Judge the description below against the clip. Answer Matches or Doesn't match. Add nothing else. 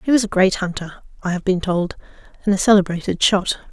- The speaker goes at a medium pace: Doesn't match